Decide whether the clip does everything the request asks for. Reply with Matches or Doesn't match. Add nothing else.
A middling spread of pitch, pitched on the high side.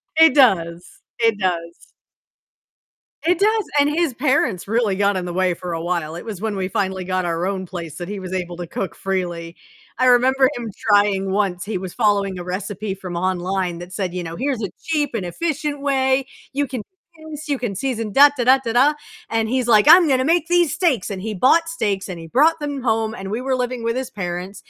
Doesn't match